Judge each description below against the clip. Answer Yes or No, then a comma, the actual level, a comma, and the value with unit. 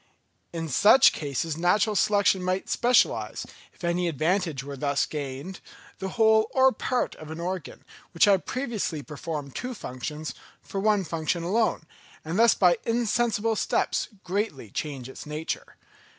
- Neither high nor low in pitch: Yes, medium, 180 Hz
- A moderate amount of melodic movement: No, wide, 5.8 semitones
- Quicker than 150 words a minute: No, average, 145 wpm